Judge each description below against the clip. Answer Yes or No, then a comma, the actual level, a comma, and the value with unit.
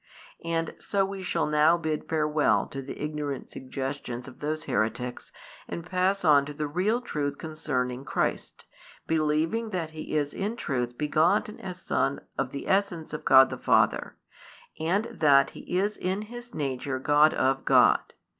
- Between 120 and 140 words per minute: No, average, 160 wpm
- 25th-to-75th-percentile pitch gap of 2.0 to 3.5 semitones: No, average, 4.7 semitones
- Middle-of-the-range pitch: Yes, medium, 155 Hz